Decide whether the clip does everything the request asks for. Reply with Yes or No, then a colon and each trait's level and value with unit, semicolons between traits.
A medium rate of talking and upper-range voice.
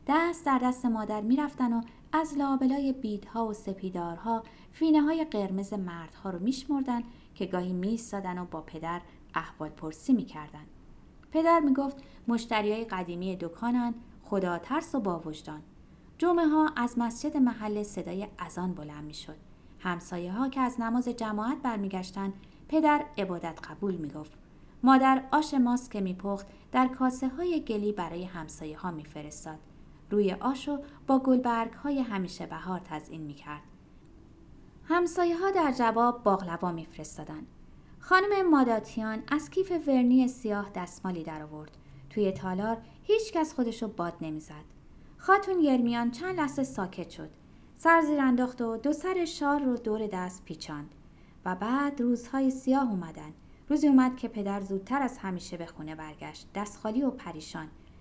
Yes: average, 140 wpm; high, 220 Hz